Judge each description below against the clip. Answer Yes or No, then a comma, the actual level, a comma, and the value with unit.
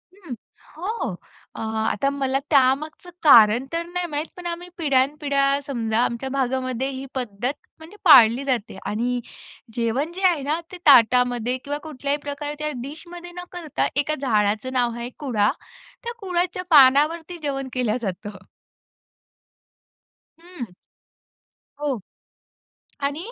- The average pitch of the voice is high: Yes, very high, 275 Hz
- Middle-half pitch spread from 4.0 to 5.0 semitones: Yes, average, 4.3 semitones